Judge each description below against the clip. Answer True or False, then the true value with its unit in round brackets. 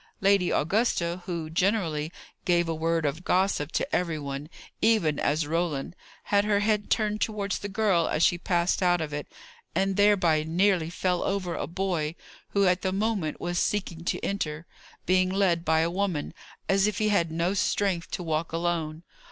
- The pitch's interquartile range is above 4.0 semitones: False (3.5 semitones)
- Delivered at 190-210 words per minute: False (175 wpm)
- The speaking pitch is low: False (175 Hz)